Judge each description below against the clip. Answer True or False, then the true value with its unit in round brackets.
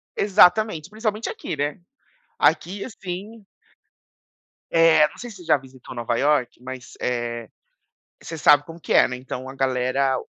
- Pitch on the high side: False (150 Hz)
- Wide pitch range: True (6.4 semitones)